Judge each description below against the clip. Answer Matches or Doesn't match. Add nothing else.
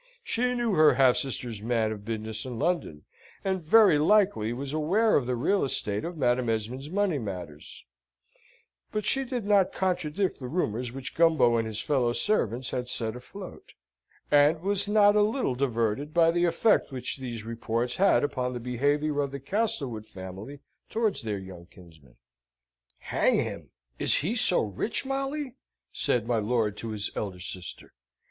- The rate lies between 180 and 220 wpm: Doesn't match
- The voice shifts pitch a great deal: Matches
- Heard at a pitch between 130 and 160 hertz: Matches